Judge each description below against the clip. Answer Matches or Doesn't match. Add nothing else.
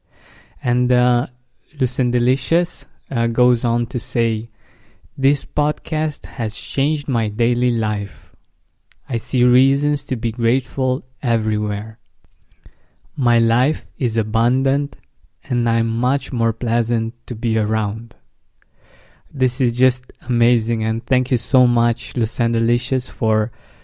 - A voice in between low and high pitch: Doesn't match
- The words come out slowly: Matches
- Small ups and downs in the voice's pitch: Matches